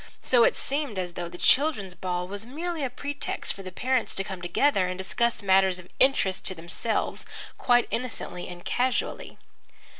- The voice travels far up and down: Yes, wide, 6.0 semitones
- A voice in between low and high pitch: No, high, 200 Hz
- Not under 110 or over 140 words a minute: No, average, 175 wpm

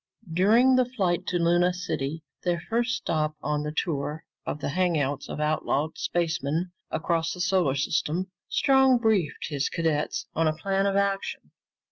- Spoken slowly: No, average, 155 wpm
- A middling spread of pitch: Yes, average, 4.1 semitones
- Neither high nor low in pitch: Yes, medium, 170 Hz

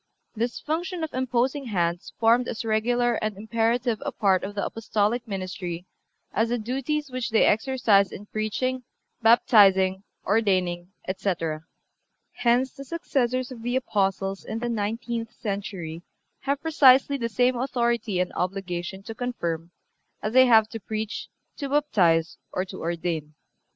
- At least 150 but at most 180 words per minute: No, average, 140 wpm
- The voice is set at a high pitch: Yes, high, 225 Hz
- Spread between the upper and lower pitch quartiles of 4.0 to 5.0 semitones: Yes, average, 4.3 semitones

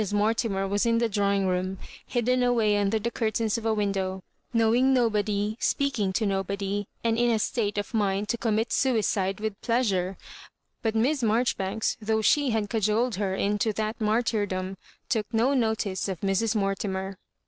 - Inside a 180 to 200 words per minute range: No, average, 160 wpm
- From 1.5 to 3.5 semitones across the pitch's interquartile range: Yes, narrow, 2.6 semitones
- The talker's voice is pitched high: Yes, high, 215 Hz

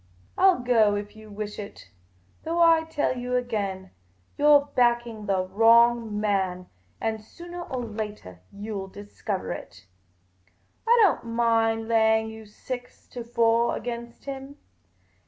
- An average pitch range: Yes, average, 3.0 semitones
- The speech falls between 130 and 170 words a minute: Yes, average, 140 wpm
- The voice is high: Yes, high, 225 Hz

